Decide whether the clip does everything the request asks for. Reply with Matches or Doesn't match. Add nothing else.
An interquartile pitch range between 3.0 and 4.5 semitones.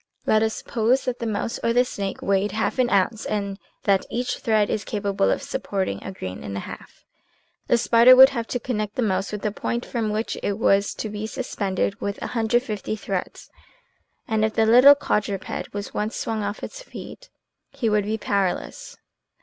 Doesn't match